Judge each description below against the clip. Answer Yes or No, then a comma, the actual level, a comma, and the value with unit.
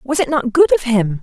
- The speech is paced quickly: Yes, fast, 295 wpm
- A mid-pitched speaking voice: No, high, 240 Hz